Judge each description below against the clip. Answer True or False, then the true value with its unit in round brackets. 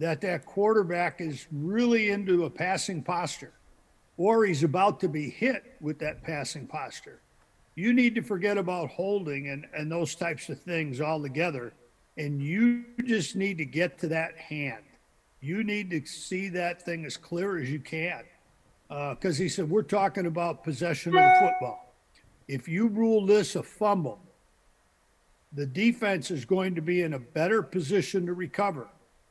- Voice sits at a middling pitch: True (175 Hz)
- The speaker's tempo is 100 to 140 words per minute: False (170 wpm)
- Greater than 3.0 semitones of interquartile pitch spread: True (4.5 semitones)